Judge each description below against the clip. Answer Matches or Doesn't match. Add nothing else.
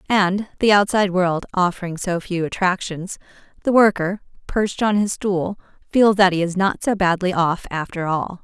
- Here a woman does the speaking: Matches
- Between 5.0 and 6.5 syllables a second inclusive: Doesn't match